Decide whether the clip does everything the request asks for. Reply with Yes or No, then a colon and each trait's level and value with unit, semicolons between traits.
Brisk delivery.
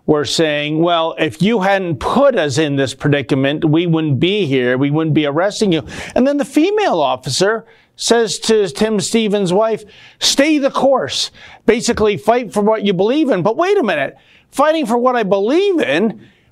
No: average, 180 wpm